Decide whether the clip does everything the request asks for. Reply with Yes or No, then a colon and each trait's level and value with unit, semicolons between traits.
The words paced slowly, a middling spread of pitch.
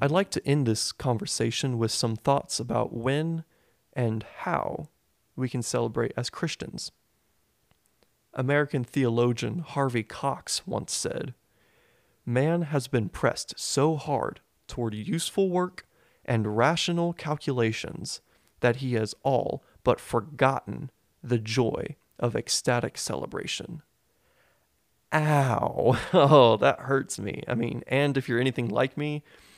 Yes: slow, 120 wpm; average, 4.0 semitones